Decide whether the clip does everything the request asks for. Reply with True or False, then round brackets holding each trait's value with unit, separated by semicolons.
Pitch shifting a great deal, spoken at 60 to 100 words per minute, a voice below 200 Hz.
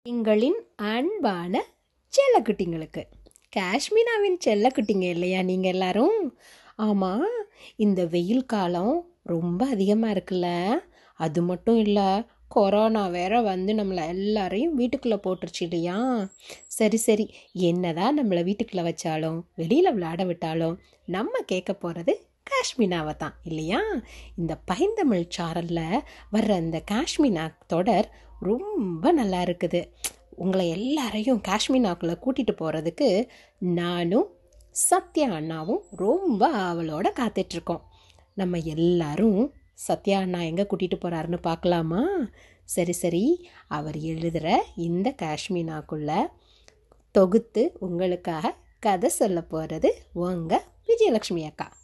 True (6.2 semitones; 95 wpm; 190 Hz)